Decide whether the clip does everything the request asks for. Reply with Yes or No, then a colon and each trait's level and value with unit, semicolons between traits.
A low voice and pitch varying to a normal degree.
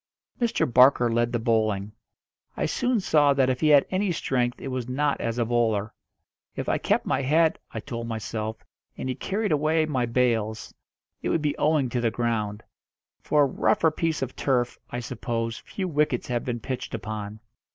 Yes: low, 125 Hz; average, 4.4 semitones